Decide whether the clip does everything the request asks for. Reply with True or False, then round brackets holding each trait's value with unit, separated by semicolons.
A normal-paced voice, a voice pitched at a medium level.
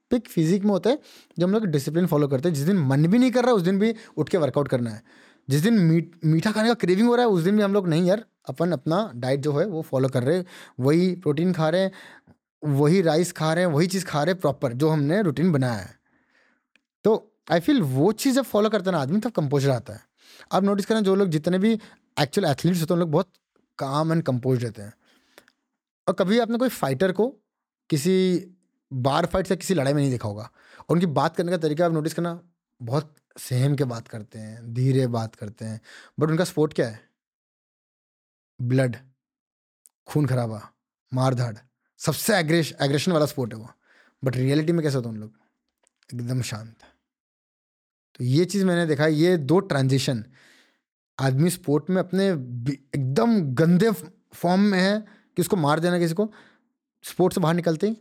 False (200 wpm; 165 Hz)